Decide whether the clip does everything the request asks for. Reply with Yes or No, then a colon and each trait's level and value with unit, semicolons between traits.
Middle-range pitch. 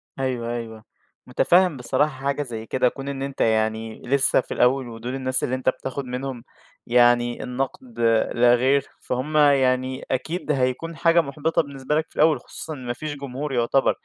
No: low, 130 Hz